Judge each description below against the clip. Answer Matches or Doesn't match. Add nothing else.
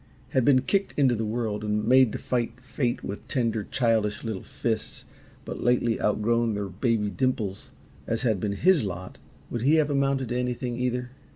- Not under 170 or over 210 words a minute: Matches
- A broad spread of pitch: Doesn't match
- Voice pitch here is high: Doesn't match